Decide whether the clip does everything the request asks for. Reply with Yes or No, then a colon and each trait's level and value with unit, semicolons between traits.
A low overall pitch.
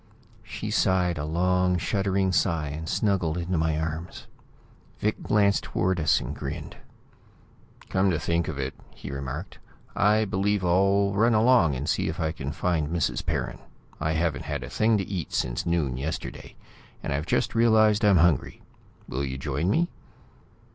Yes: very low, 85 Hz